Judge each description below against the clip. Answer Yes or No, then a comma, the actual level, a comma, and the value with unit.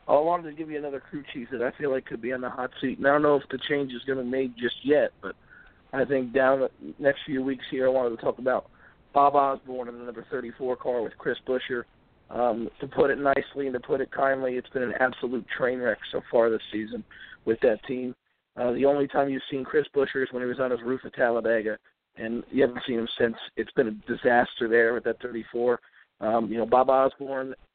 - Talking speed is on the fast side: Yes, fast, 250 wpm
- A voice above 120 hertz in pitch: Yes, low, 130 Hz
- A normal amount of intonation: No, narrow, 2.3 semitones